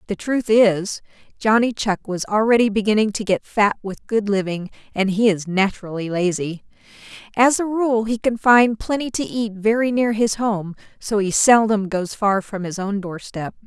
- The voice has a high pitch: Yes, high, 210 Hz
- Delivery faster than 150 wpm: Yes, average, 180 wpm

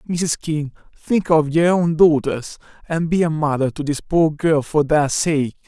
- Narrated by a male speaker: Yes, male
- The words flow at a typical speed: Yes, average, 190 wpm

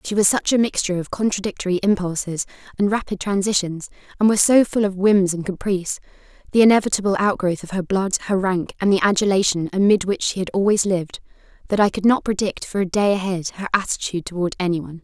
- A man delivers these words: No, female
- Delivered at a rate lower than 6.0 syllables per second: No, 6.3 syllables/s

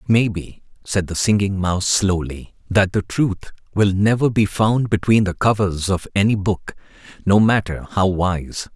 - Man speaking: Yes, male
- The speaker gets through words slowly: No, average, 170 wpm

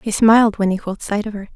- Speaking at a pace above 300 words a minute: Yes, fast, 310 wpm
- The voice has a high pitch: Yes, high, 210 Hz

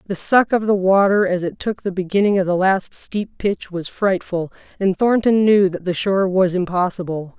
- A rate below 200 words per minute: No, fast, 205 wpm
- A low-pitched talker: No, high, 190 Hz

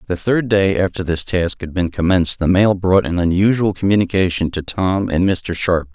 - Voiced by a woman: No, male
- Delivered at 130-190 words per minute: No, average, 200 wpm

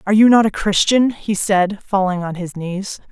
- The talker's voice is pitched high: Yes, high, 200 Hz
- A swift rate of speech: Yes, fast, 210 wpm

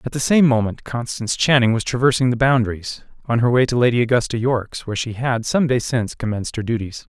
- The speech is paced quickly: Yes, fast, 220 wpm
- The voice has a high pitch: No, low, 120 Hz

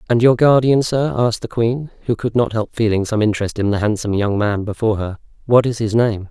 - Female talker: No, male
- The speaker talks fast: Yes, fast, 240 wpm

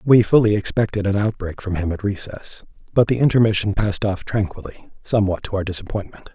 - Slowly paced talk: No, average, 180 wpm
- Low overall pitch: Yes, low, 100 Hz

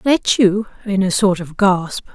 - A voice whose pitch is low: No, high, 195 Hz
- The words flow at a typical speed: Yes, average, 195 wpm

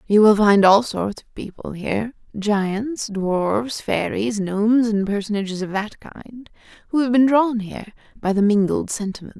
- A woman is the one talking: Yes, female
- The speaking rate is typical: Yes, average, 185 wpm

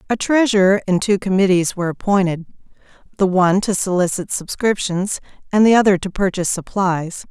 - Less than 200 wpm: Yes, average, 150 wpm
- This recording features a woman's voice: Yes, female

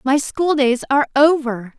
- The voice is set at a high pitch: Yes, very high, 275 Hz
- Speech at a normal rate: Yes, average, 170 wpm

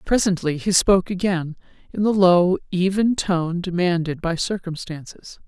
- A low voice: No, medium, 180 Hz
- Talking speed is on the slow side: Yes, slow, 130 wpm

